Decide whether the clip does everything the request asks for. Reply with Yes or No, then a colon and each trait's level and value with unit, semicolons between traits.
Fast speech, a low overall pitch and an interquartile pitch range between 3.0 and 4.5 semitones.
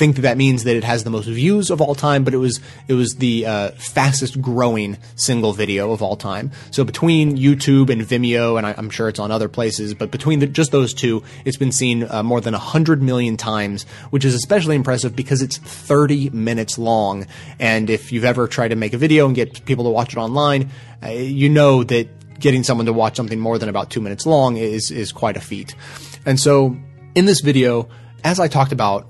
Yes: fast, 225 wpm; low, 125 Hz; average, 3.3 semitones